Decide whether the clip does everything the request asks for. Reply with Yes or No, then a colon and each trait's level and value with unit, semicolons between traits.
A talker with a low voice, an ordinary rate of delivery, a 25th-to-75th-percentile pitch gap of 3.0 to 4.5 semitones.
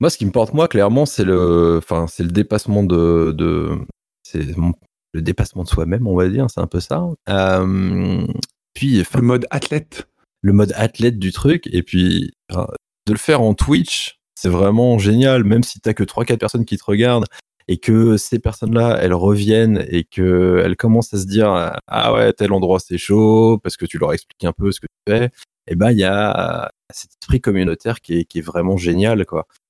Yes: low, 100 Hz; average, 205 wpm; average, 4.1 semitones